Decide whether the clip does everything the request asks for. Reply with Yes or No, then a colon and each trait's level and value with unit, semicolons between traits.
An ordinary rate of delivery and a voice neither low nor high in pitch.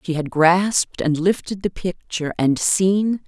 Yes: average, 165 wpm; medium, 175 Hz